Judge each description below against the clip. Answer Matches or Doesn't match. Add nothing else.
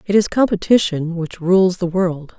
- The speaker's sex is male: Doesn't match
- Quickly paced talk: Doesn't match